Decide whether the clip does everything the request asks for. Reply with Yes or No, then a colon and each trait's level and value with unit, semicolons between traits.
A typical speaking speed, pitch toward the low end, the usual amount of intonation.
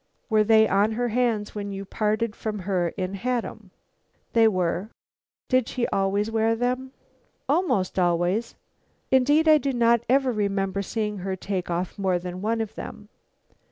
No: average, 160 wpm; high, 215 Hz; average, 3.4 semitones